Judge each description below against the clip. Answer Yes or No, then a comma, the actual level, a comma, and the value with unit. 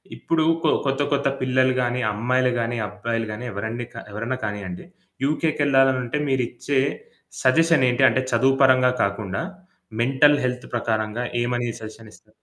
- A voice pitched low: Yes, low, 125 Hz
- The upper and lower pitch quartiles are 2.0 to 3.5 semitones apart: Yes, average, 2.8 semitones